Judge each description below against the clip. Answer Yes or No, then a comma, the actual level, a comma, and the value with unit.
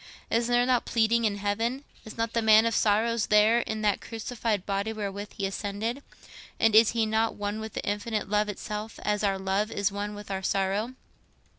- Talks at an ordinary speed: Yes, average, 190 wpm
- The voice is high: Yes, high, 215 Hz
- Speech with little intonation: Yes, narrow, 1.9 semitones